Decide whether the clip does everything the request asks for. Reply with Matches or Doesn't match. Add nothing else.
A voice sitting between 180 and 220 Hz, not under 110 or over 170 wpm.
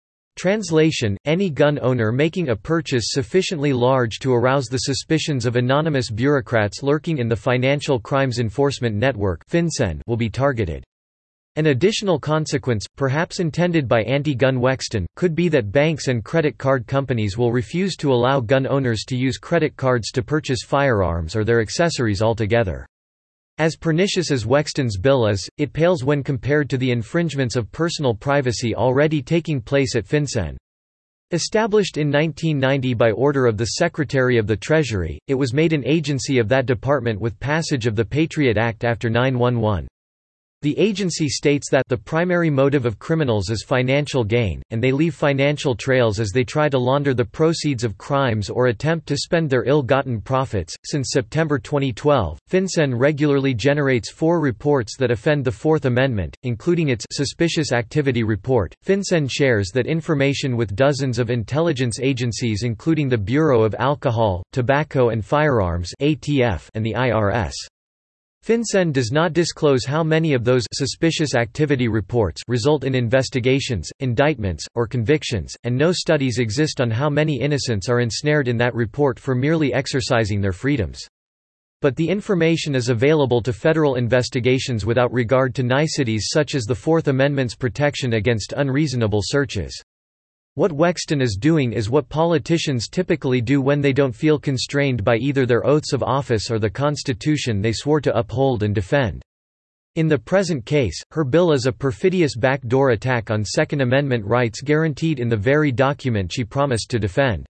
Doesn't match